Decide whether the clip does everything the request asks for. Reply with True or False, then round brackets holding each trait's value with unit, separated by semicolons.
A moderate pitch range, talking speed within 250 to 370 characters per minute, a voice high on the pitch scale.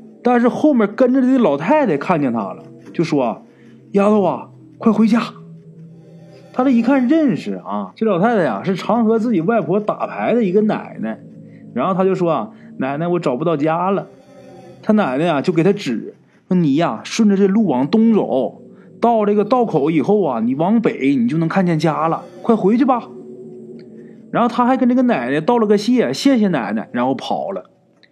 True (4.4 semitones; 270 characters per minute; 215 Hz)